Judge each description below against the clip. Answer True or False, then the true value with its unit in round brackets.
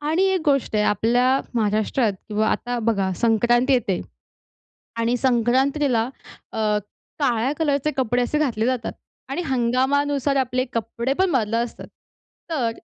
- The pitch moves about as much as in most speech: True (3.3 semitones)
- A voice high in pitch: True (245 Hz)